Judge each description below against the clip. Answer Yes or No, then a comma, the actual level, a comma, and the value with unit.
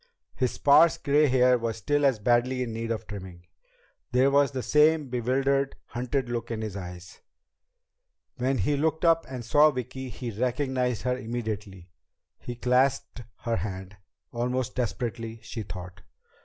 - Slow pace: No, average, 150 wpm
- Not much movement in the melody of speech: No, average, 3.2 semitones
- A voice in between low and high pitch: No, low, 125 Hz